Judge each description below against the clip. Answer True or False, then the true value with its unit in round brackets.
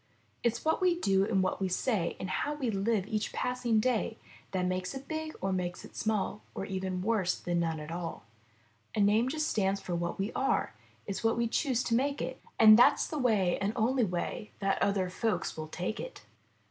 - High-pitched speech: True (210 Hz)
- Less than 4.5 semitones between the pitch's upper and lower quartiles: False (4.8 semitones)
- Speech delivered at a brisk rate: True (210 wpm)